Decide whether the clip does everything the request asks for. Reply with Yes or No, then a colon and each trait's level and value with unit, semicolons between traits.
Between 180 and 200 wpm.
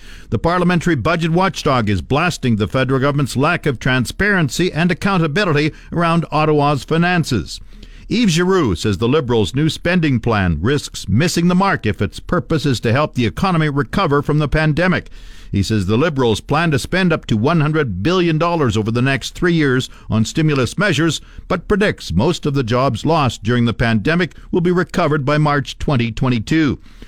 No: average, 170 wpm